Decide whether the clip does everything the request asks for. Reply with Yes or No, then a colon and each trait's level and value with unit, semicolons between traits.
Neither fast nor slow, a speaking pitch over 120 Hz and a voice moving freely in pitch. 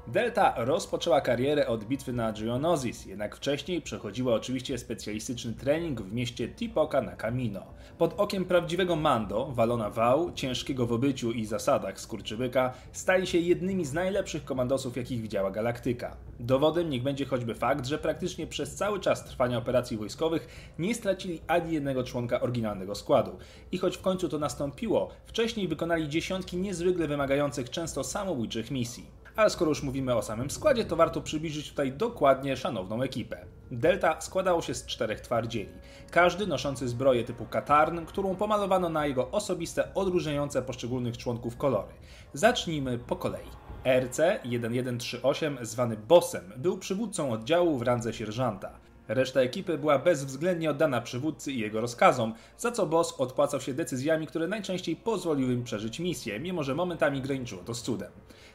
Yes: average, 150 wpm; medium, 140 Hz; wide, 5.9 semitones